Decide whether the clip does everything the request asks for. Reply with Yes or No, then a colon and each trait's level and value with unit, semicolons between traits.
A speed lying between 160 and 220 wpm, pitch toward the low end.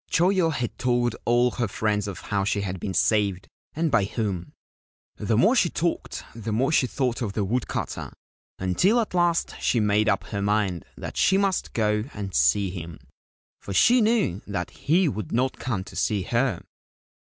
Yes: average, 185 wpm; low, 110 Hz